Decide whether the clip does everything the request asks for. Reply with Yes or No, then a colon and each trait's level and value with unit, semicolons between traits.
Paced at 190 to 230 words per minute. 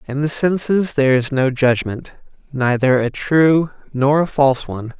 No: average, 155 wpm